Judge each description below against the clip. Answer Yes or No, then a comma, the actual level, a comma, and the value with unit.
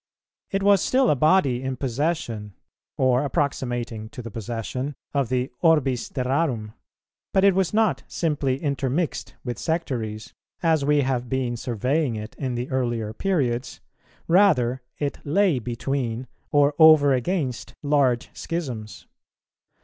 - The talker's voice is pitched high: No, low, 130 Hz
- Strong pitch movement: No, average, 4.5 semitones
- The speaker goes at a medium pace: No, slow, 130 wpm